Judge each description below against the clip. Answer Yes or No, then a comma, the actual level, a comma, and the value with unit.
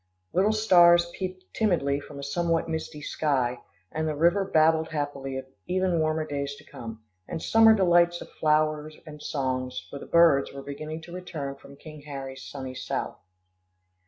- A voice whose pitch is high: No, medium, 155 Hz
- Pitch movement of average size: Yes, average, 3.5 semitones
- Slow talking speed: No, average, 165 wpm